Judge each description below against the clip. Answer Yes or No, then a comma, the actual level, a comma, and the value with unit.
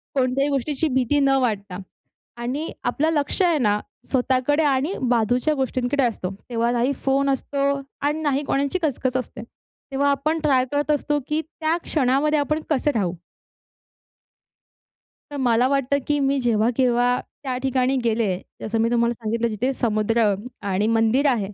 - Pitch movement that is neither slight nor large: Yes, average, 3.4 semitones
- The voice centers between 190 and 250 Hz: No, very high, 260 Hz